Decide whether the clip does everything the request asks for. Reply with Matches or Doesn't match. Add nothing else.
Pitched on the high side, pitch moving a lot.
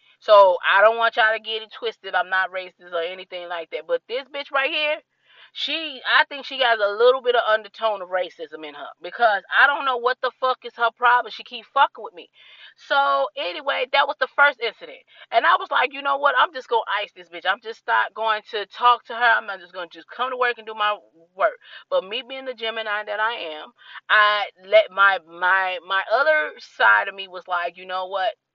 Matches